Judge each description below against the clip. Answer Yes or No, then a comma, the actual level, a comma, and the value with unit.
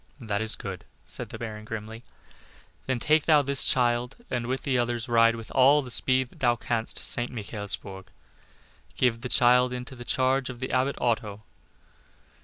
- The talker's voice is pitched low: Yes, low, 120 Hz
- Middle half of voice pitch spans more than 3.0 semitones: No, narrow, 2.4 semitones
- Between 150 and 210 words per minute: Yes, average, 180 wpm